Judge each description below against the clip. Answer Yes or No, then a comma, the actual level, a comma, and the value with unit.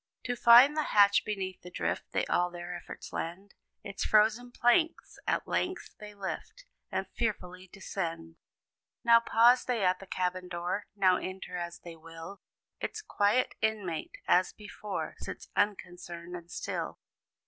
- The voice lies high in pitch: Yes, high, 195 Hz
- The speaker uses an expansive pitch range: No, average, 3.9 semitones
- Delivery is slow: No, average, 150 wpm